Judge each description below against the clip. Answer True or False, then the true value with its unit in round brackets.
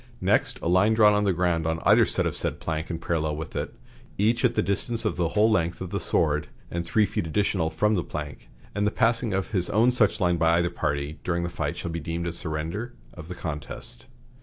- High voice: False (85 Hz)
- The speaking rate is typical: False (235 wpm)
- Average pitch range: True (4.4 semitones)